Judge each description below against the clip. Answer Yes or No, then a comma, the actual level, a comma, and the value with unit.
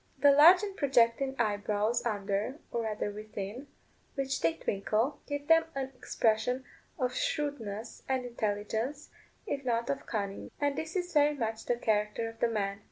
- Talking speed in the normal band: Yes, average, 160 wpm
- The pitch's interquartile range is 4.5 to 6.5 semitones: Yes, average, 4.8 semitones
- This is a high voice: Yes, high, 235 Hz